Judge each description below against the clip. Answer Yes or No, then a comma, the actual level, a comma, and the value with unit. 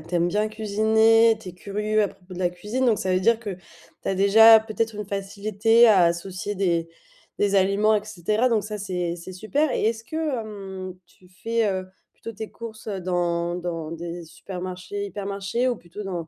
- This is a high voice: Yes, high, 200 Hz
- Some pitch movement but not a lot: Yes, average, 3.2 semitones